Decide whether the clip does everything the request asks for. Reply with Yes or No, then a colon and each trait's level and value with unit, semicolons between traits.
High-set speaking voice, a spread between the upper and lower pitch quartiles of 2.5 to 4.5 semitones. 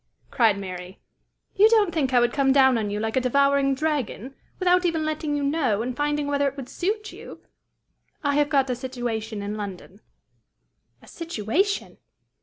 No: very high, 270 Hz; average, 5.3 semitones